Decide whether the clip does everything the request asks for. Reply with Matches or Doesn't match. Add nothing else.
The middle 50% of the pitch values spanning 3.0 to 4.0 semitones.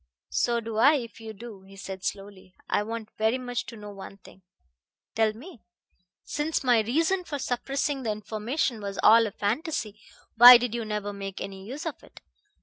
Matches